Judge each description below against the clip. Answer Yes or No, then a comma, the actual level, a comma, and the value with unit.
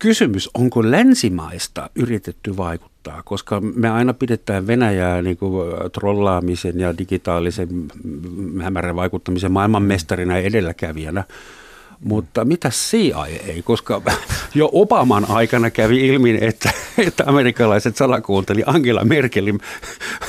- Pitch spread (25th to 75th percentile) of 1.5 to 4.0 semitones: No, average, 4.6 semitones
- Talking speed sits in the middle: Yes, average, 110 wpm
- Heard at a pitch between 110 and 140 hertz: No, low, 100 Hz